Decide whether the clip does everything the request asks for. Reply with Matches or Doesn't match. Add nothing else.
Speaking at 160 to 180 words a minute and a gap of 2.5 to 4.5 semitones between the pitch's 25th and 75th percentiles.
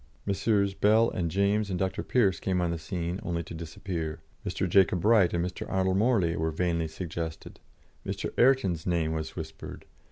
Matches